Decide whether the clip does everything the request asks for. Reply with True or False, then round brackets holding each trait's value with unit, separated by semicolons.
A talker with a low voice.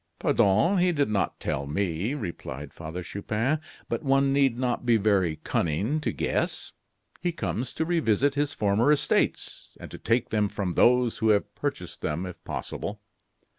True (115 Hz)